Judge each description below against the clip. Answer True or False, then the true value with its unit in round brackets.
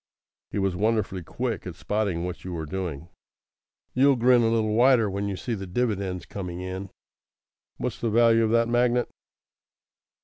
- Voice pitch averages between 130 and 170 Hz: False (105 Hz)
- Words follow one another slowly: False (165 wpm)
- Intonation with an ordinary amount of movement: True (4.1 semitones)